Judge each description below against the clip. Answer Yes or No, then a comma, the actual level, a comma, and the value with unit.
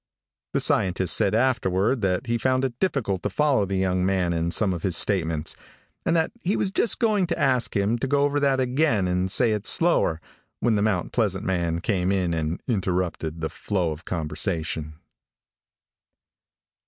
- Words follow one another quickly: No, average, 180 wpm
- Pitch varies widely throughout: Yes, wide, 6.4 semitones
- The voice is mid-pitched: No, low, 100 Hz